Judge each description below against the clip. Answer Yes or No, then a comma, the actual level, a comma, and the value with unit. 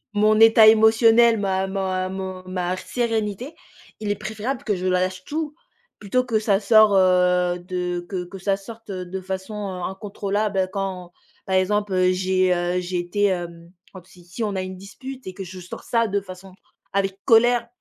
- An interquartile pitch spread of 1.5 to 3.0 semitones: Yes, average, 2.7 semitones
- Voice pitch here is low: No, high, 195 Hz